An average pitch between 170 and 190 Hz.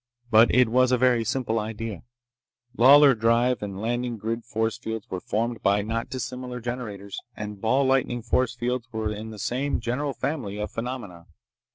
No: low, 115 Hz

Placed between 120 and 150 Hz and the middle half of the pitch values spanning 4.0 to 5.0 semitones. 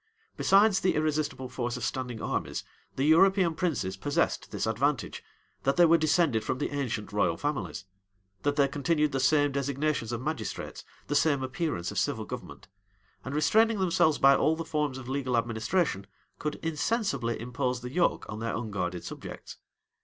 Yes: medium, 140 Hz; average, 4.5 semitones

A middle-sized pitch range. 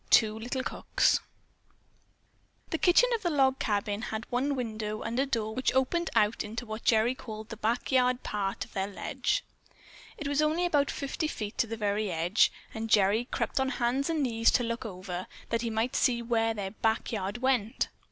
Yes: average, 3.5 semitones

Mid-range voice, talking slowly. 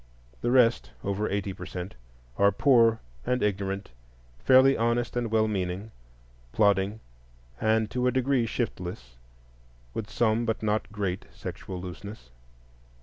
No: low, 105 Hz; slow, 130 wpm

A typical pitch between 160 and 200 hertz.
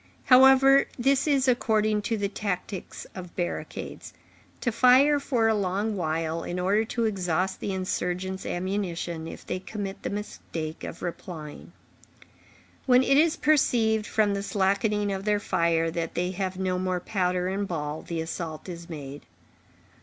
Yes: high, 190 Hz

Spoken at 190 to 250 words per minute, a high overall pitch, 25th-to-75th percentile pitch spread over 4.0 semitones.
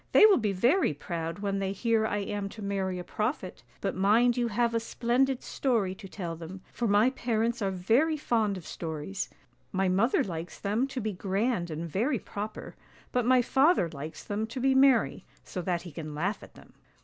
Yes: average, 200 wpm; high, 205 Hz; average, 4.6 semitones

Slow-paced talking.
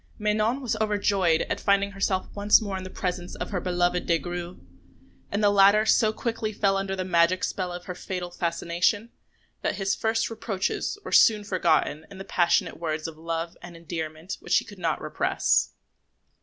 No: average, 185 wpm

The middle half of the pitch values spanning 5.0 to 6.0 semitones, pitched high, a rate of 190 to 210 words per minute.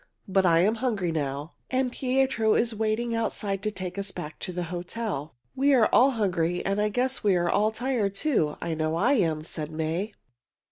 Yes: average, 5.3 semitones; high, 200 Hz; average, 195 wpm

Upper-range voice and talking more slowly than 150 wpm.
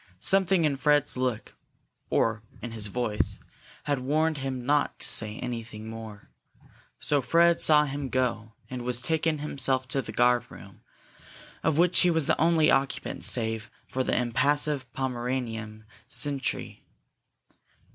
No: low, 130 Hz; average, 140 wpm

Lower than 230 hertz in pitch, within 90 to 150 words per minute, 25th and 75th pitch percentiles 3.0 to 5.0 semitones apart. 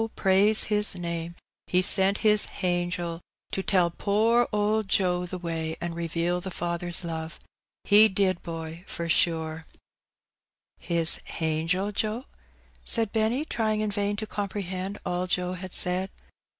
Yes: medium, 185 Hz; average, 145 wpm; average, 3.3 semitones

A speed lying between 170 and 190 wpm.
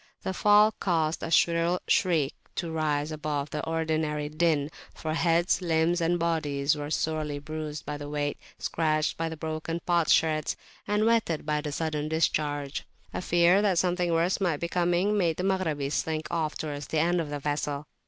Yes: average, 175 wpm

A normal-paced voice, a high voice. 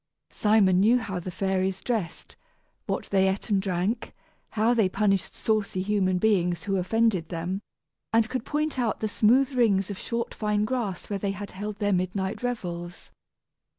Yes: average, 165 wpm; high, 200 Hz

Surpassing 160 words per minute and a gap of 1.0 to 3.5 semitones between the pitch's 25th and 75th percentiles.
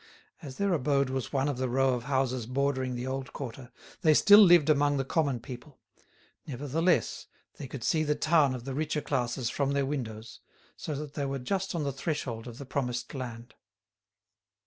Yes: average, 190 wpm; average, 2.9 semitones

